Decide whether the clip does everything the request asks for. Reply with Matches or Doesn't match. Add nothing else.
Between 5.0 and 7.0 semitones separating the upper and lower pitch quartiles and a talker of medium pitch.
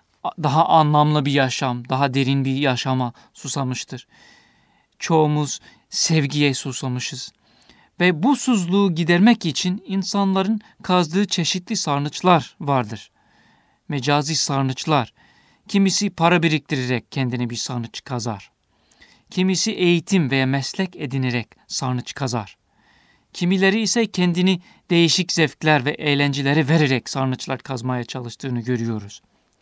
Matches